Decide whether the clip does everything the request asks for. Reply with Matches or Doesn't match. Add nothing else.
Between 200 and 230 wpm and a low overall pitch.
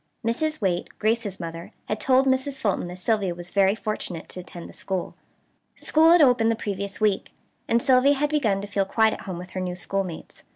Doesn't match